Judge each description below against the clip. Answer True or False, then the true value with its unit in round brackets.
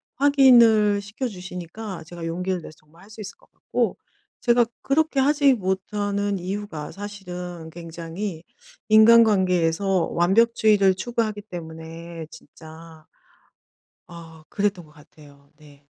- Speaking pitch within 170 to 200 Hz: True (190 Hz)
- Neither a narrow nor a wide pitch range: True (4.4 semitones)